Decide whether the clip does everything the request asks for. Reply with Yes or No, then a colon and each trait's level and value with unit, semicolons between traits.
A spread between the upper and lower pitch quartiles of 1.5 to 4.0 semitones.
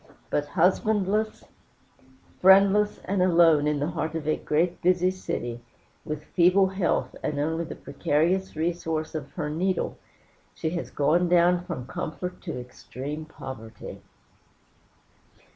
Yes: average, 3.4 semitones